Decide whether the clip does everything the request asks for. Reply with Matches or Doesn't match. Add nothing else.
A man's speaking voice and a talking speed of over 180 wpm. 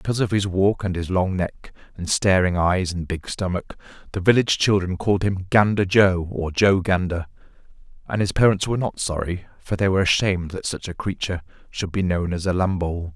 Matches